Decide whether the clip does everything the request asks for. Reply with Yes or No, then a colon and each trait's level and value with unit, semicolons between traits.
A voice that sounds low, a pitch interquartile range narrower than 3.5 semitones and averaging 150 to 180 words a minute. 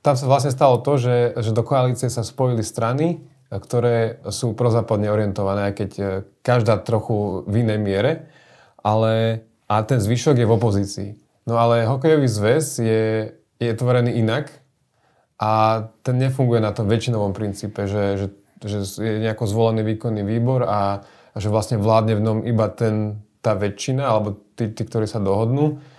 Yes: low, 115 Hz; narrow, 2.6 semitones; average, 160 wpm